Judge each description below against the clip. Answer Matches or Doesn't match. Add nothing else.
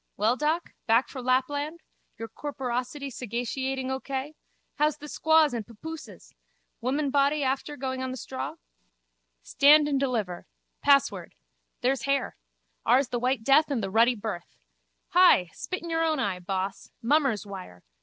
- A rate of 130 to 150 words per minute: Matches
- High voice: Matches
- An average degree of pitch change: Matches